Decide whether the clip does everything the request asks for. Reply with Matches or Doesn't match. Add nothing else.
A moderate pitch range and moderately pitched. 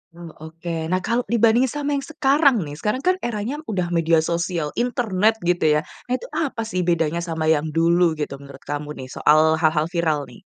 Doesn't match